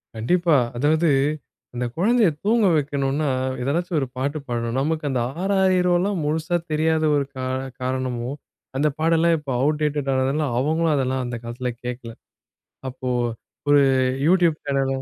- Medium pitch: Yes, medium, 150 Hz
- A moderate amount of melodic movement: Yes, average, 4.2 semitones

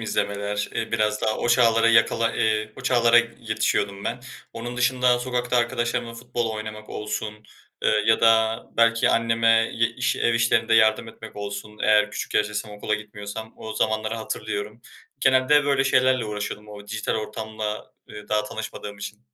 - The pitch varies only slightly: Yes, narrow, 1.8 semitones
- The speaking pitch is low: Yes, low, 110 Hz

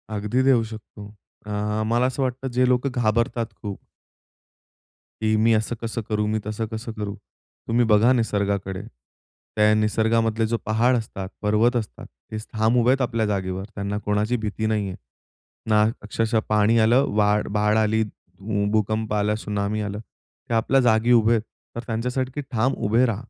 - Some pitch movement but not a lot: No, narrow, 1.9 semitones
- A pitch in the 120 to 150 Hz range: No, low, 110 Hz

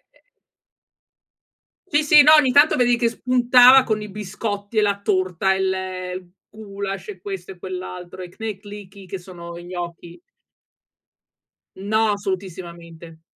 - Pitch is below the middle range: No, high, 195 Hz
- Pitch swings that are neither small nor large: Yes, average, 3.1 semitones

